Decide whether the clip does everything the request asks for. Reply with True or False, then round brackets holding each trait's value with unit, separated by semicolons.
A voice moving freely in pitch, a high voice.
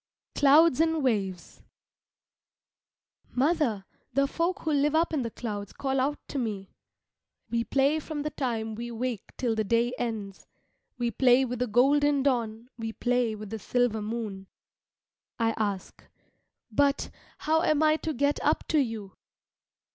False (4.5 semitones; 245 Hz)